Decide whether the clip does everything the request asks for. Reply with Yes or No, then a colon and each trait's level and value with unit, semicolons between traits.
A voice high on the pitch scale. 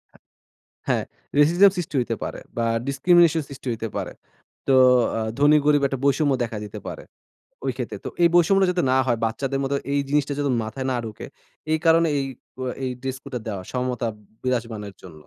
No: low, 135 Hz